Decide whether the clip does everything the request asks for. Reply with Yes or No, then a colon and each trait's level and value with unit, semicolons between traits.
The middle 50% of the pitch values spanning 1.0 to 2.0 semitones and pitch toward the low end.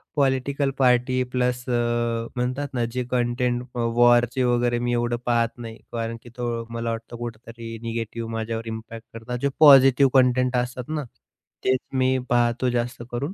Yes: narrow, 1.6 semitones; low, 120 Hz